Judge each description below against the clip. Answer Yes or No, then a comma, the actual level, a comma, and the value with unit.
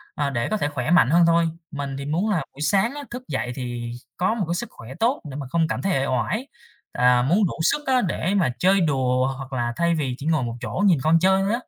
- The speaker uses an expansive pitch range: Yes, wide, 6.6 semitones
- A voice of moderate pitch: Yes, medium, 160 Hz